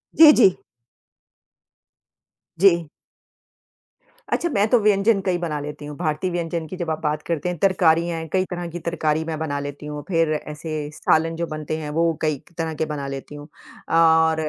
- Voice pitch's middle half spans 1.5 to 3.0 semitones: Yes, narrow, 2.5 semitones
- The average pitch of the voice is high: No, medium, 160 Hz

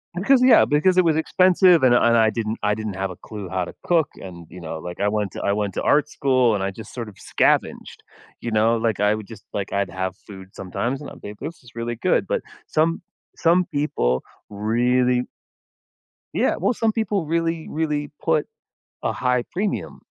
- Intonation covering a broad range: Yes, wide, 7.6 semitones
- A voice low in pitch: Yes, low, 120 Hz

